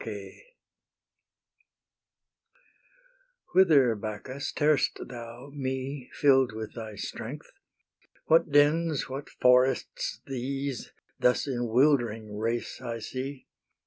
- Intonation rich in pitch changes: No, average, 3.2 semitones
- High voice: No, low, 130 Hz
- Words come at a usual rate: No, slow, 85 wpm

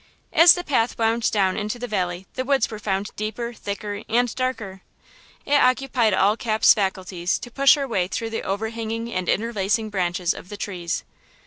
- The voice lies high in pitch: Yes, high, 215 Hz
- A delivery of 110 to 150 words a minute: No, average, 180 wpm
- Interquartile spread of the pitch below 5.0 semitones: Yes, average, 3.7 semitones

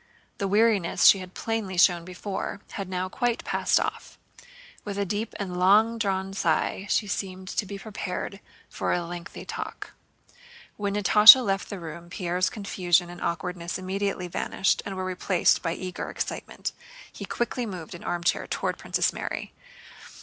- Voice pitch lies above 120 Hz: Yes, high, 190 Hz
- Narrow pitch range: Yes, narrow, 2.2 semitones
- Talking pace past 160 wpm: No, average, 155 wpm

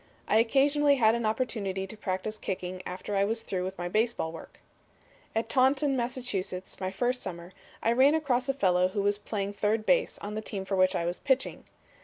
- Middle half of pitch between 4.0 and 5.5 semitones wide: Yes, average, 4.9 semitones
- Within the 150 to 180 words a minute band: No, average, 200 wpm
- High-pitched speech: Yes, high, 215 Hz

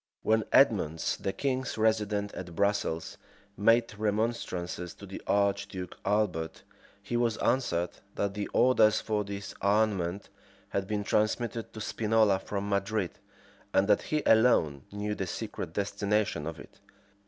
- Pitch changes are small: Yes, narrow, 2.3 semitones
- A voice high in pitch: No, low, 105 Hz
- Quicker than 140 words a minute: No, slow, 135 wpm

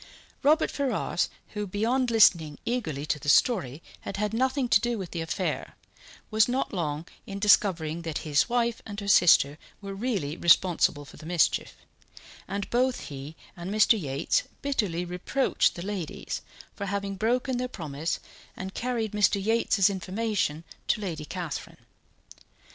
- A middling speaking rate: Yes, average, 150 wpm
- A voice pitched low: No, high, 195 Hz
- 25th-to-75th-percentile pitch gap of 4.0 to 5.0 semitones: No, wide, 5.6 semitones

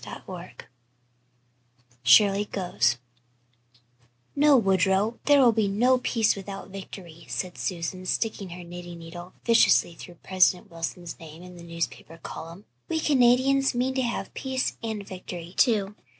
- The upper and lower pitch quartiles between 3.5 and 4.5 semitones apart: No, average, 5.3 semitones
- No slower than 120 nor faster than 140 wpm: Yes, slow, 135 wpm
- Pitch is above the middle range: Yes, high, 195 Hz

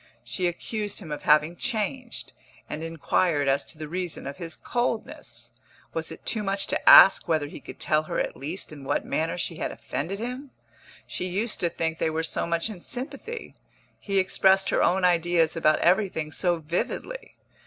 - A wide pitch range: No, average, 3.9 semitones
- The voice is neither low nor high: Yes, medium, 175 Hz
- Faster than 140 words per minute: Yes, average, 185 wpm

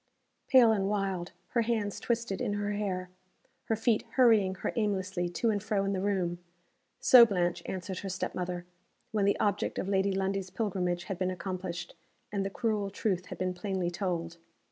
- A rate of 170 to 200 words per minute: Yes, average, 180 wpm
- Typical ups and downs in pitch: No, narrow, 2.3 semitones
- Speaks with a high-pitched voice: Yes, high, 195 Hz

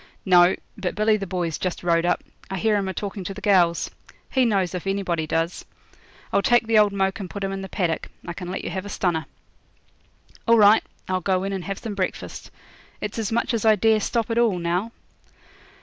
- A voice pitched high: Yes, high, 195 Hz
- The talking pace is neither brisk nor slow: No, fast, 220 wpm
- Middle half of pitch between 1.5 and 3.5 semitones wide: Yes, average, 2.9 semitones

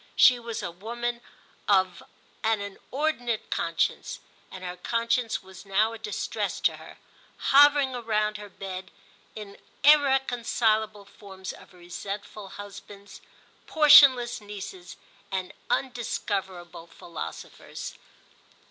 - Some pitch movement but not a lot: Yes, average, 3.8 semitones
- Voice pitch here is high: Yes, high, 210 Hz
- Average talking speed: No, slow, 105 wpm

